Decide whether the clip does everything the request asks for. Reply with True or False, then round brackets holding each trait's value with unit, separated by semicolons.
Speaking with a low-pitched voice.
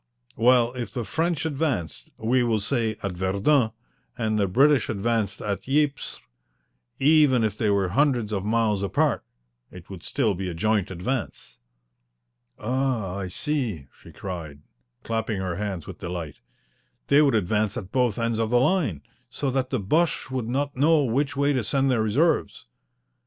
True (115 Hz)